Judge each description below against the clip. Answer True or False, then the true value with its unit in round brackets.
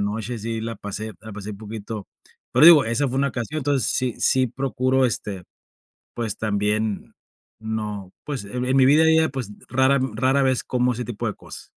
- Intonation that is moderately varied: True (3.7 semitones)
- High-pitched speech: False (115 Hz)